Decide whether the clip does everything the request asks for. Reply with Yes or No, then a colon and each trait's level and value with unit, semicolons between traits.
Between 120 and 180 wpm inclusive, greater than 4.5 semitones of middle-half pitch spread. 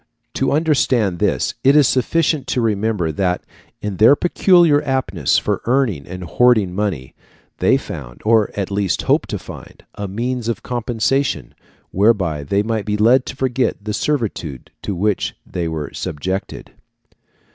Yes: average, 150 wpm; wide, 5.6 semitones